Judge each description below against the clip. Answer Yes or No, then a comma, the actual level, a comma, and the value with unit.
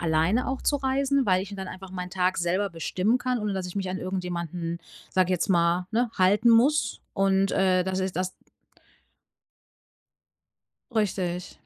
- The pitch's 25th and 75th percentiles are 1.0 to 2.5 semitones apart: No, average, 2.9 semitones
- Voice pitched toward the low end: No, high, 190 Hz